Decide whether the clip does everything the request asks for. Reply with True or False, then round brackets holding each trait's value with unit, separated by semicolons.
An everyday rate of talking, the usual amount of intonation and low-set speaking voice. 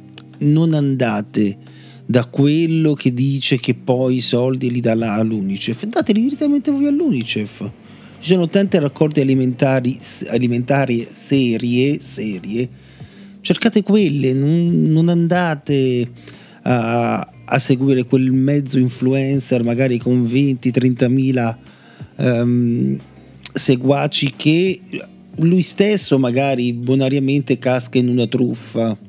False (105 wpm; 3.5 semitones; 130 Hz)